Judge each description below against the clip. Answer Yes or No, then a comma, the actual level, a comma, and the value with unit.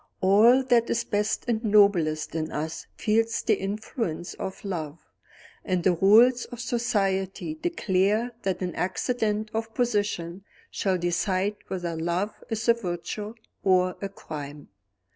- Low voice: No, high, 200 Hz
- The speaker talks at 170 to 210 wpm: No, slow, 135 wpm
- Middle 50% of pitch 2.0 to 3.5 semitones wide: No, average, 4.1 semitones